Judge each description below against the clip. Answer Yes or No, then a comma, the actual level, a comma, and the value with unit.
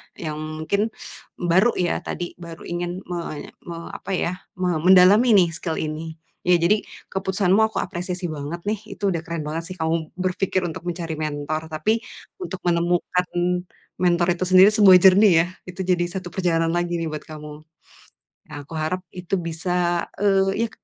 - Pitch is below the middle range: No, medium, 175 Hz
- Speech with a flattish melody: Yes, narrow, 2.3 semitones